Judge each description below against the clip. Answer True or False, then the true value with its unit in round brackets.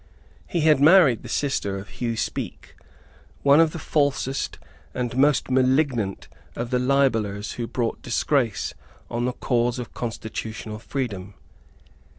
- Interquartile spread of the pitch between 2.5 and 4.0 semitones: True (3.6 semitones)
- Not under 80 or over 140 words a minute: True (135 wpm)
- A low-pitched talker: True (125 Hz)